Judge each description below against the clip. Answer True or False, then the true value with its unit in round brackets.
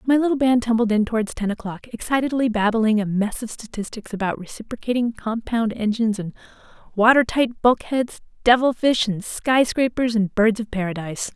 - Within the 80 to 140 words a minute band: False (160 wpm)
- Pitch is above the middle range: True (225 Hz)